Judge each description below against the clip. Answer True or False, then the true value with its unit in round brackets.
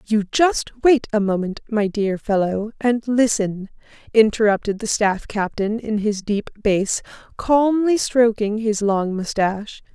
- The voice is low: False (215 Hz)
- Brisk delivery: False (140 wpm)